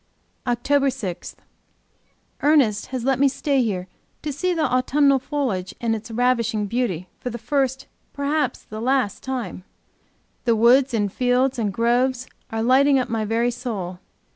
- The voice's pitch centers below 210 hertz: No, high, 245 Hz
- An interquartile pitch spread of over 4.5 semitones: No, average, 3.3 semitones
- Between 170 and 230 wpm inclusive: No, average, 155 wpm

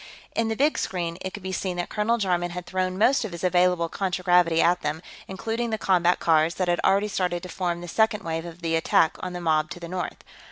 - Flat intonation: Yes, narrow, 2.0 semitones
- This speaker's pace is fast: Yes, fast, 240 wpm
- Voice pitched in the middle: Yes, medium, 180 Hz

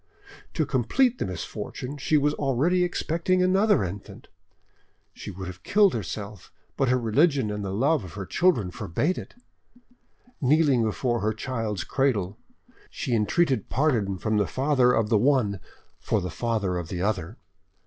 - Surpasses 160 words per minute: No, average, 155 wpm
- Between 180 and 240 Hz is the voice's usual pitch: No, low, 120 Hz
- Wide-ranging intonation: Yes, wide, 6.5 semitones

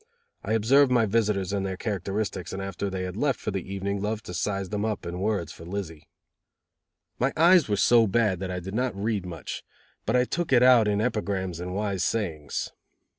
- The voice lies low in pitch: Yes, low, 100 Hz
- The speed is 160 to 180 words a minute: No, fast, 205 wpm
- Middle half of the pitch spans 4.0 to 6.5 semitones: No, average, 3.2 semitones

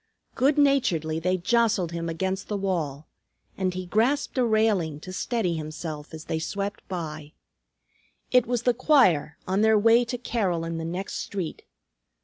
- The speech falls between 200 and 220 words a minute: No, average, 160 wpm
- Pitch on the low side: No, medium, 185 Hz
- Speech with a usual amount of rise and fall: No, wide, 5.8 semitones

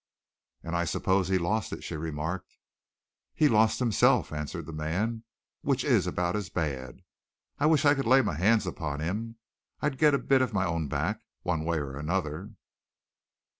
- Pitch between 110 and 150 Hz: No, very low, 90 Hz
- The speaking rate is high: No, average, 175 wpm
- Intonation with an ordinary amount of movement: No, wide, 6.0 semitones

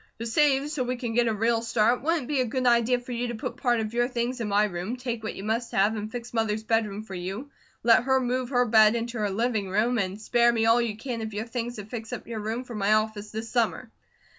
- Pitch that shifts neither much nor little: No, narrow, 2.2 semitones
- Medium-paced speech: No, fast, 270 wpm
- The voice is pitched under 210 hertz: No, high, 230 Hz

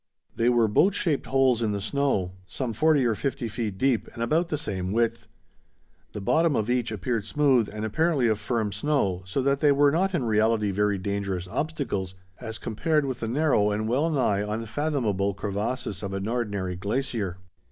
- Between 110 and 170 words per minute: No, average, 180 wpm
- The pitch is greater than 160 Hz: No, low, 115 Hz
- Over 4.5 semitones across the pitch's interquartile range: Yes, average, 5.1 semitones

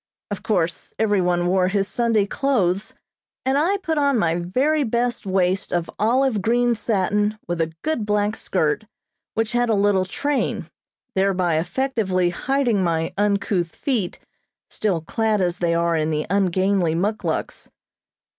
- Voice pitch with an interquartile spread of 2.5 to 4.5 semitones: No, average, 4.9 semitones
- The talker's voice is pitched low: No, high, 200 Hz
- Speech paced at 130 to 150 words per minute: Yes, average, 145 wpm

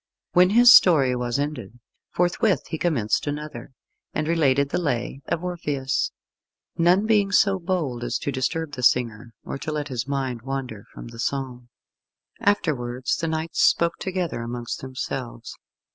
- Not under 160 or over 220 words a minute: No, average, 150 wpm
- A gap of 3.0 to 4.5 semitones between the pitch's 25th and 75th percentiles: No, wide, 5.6 semitones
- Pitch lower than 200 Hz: Yes, medium, 140 Hz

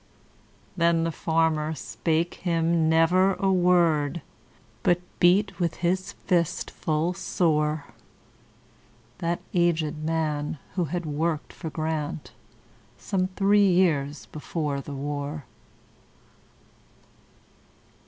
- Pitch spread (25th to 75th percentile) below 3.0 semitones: Yes, narrow, 2.6 semitones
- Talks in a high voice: No, medium, 165 Hz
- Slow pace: Yes, slow, 85 wpm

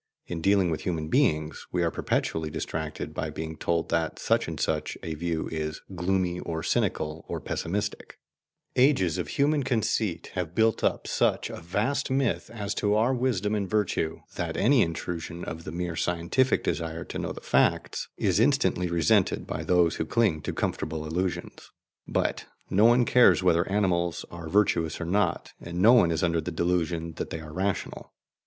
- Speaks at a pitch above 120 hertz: No, very low, 90 Hz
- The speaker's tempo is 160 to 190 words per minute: Yes, average, 175 wpm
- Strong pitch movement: No, average, 4.1 semitones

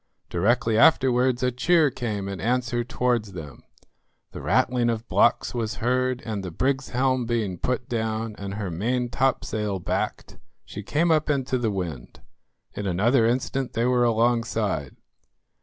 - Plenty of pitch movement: No, average, 3.3 semitones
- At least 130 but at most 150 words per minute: Yes, average, 145 wpm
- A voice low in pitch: Yes, low, 120 Hz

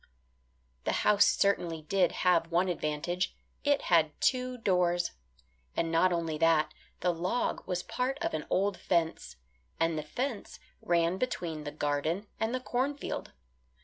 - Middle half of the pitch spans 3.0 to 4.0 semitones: Yes, average, 3.7 semitones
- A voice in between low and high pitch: Yes, medium, 175 Hz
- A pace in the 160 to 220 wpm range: No, average, 145 wpm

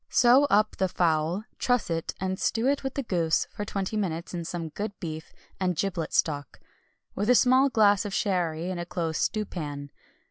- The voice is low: No, medium, 185 Hz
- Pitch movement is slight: No, average, 4.6 semitones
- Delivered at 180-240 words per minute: Yes, average, 185 wpm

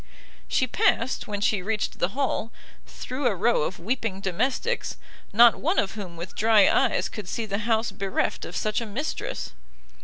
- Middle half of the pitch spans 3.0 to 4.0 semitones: Yes, average, 3.4 semitones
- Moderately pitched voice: No, high, 220 Hz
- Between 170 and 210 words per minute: Yes, average, 175 wpm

